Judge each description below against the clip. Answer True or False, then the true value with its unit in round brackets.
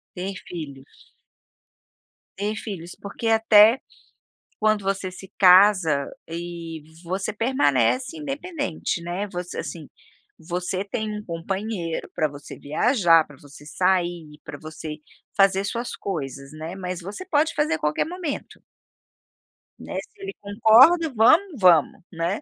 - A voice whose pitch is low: False (190 Hz)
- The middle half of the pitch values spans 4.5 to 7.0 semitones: True (5.1 semitones)